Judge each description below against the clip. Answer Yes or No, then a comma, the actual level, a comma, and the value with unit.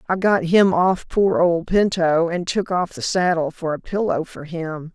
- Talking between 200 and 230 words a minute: Yes, fast, 205 wpm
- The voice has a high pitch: No, medium, 175 Hz